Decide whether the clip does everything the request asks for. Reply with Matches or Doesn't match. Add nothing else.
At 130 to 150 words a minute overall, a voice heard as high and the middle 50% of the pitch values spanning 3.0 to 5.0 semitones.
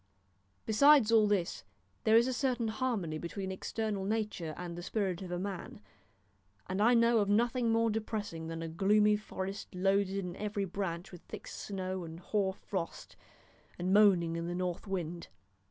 Doesn't match